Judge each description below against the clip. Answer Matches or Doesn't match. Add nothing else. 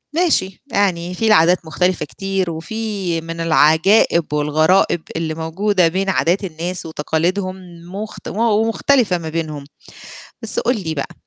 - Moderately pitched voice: Matches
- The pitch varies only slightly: Doesn't match